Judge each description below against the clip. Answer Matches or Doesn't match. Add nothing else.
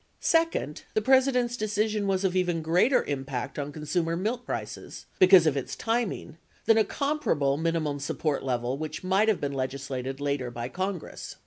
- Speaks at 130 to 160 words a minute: Doesn't match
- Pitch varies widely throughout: Matches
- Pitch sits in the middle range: Matches